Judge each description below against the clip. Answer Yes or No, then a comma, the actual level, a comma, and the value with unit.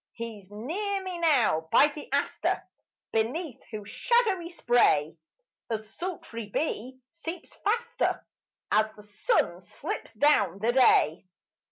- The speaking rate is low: Yes, slow, 120 wpm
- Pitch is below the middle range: No, very high, 255 Hz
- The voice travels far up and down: Yes, wide, 8.2 semitones